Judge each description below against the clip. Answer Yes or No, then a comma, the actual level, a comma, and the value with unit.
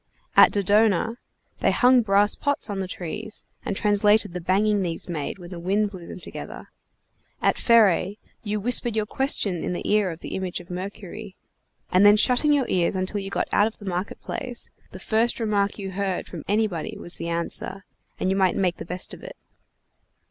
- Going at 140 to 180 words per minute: No, average, 195 wpm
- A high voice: Yes, high, 200 Hz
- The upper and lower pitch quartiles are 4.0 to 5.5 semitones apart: No, average, 2.7 semitones